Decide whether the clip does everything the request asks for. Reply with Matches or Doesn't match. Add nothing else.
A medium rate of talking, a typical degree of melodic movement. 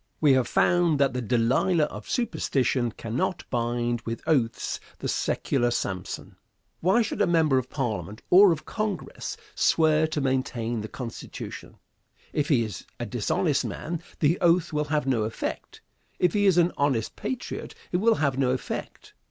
Doesn't match